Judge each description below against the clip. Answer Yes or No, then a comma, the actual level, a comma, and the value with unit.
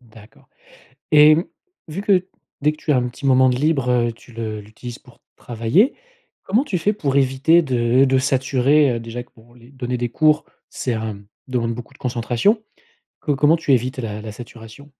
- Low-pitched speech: Yes, low, 130 Hz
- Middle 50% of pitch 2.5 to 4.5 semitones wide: Yes, average, 4.0 semitones